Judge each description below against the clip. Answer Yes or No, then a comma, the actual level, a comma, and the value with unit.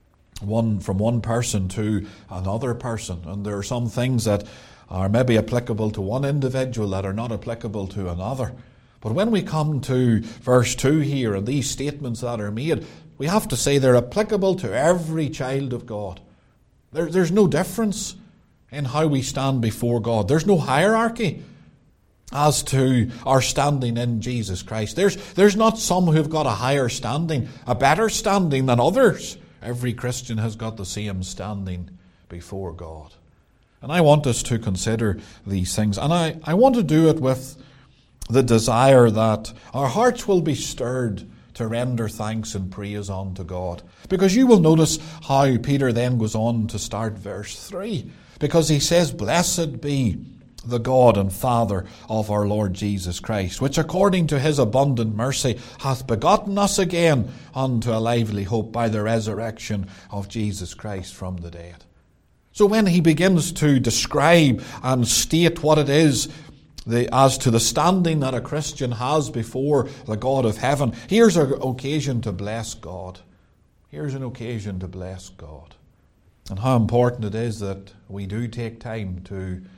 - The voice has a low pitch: Yes, low, 120 Hz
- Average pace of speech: Yes, average, 165 wpm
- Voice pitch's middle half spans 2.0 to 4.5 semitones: No, wide, 5.5 semitones